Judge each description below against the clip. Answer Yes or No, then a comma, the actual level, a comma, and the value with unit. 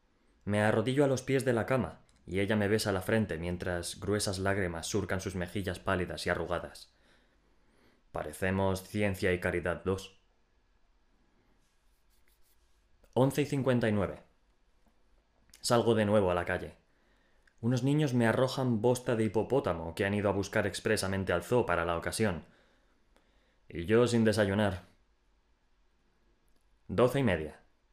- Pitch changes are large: No, average, 4.2 semitones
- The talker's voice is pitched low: Yes, low, 100 Hz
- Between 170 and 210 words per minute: No, average, 135 wpm